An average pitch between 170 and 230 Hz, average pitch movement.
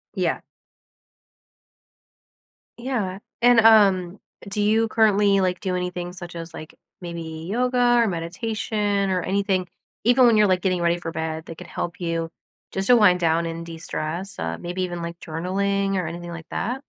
Yes: medium, 185 Hz; average, 3.5 semitones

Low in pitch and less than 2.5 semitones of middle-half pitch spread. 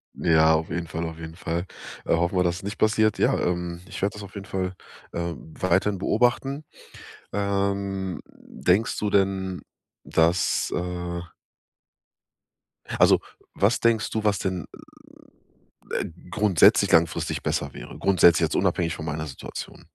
No: very low, 90 Hz; average, 2.8 semitones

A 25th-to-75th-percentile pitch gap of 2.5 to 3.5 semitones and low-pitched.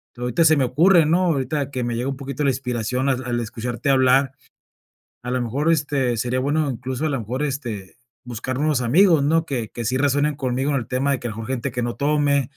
Yes: average, 2.9 semitones; low, 130 Hz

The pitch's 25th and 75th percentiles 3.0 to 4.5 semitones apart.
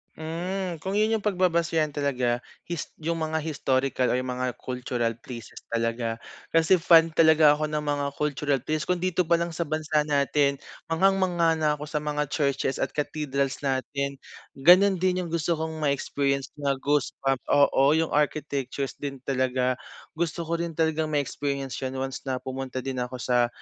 Yes: average, 3.4 semitones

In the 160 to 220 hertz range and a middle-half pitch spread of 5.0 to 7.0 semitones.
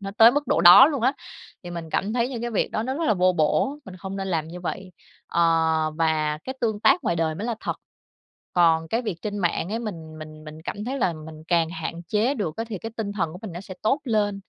Yes: high, 190 Hz; average, 5.3 semitones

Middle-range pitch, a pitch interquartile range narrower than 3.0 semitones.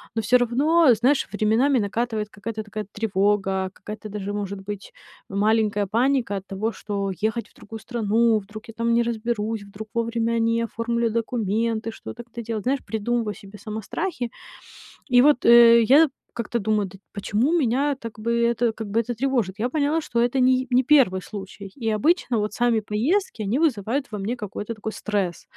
No: high, 225 Hz; narrow, 2.4 semitones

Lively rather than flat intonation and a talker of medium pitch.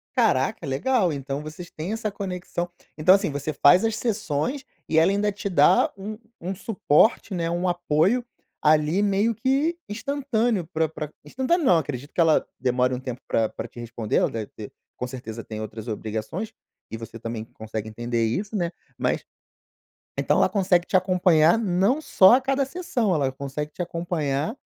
Yes: wide, 7.2 semitones; medium, 175 Hz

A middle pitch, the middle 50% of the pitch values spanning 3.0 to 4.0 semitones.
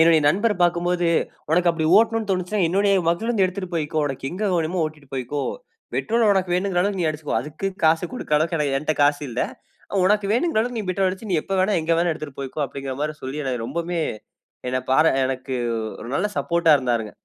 No: medium, 170 Hz; average, 4.4 semitones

